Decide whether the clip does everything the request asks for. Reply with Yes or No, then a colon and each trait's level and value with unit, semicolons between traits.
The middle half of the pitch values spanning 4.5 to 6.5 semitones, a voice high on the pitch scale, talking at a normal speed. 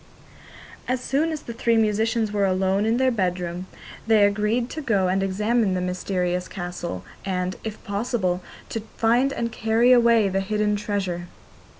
No: average, 3.8 semitones; high, 210 Hz; average, 160 wpm